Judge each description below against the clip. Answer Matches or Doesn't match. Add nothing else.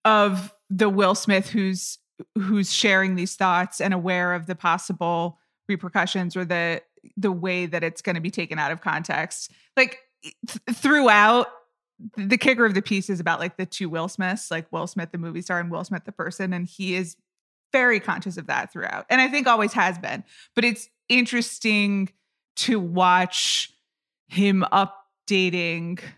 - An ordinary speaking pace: Matches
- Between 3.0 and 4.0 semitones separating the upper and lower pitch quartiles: Matches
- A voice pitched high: Matches